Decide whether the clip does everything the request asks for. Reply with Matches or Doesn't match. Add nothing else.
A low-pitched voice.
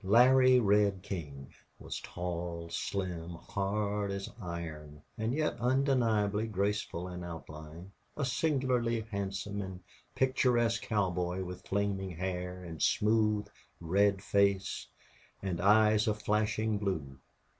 Matches